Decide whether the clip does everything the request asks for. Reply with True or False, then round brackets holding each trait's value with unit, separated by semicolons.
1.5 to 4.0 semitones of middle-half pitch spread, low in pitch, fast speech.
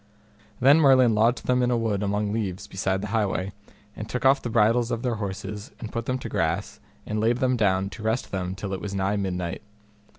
True (3.6 semitones; 105 Hz; 220 wpm)